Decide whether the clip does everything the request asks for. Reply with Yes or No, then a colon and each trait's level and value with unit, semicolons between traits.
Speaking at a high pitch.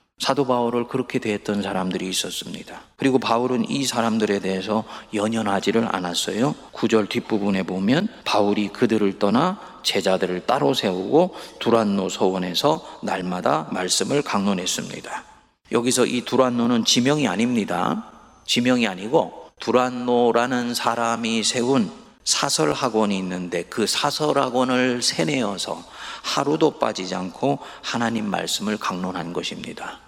No: low, 115 Hz